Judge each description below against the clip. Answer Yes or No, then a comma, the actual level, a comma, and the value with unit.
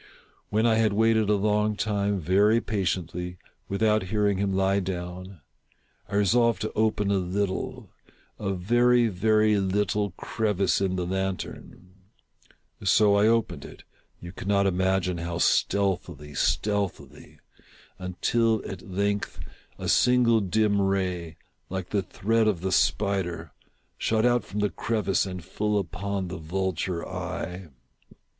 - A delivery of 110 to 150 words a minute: Yes, slow, 135 wpm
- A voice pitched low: Yes, low, 100 Hz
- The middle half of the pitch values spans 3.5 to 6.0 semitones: No, narrow, 2.5 semitones